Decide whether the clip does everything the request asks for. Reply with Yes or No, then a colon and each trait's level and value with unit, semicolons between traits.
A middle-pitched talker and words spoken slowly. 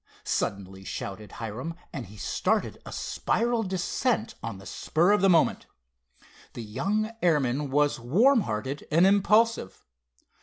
Yes: medium, 150 Hz; slow, 130 wpm